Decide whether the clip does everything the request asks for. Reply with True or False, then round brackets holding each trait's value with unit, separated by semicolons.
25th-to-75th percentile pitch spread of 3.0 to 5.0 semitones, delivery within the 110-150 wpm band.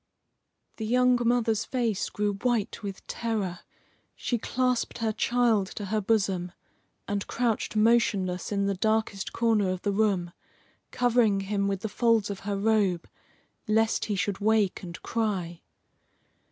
False (2.6 semitones; 140 wpm)